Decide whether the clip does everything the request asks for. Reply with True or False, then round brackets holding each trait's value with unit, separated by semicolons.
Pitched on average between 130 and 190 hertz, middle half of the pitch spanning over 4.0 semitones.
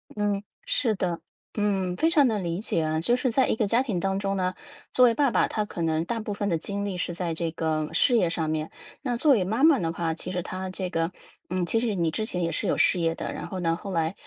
True (185 Hz; 4.7 semitones)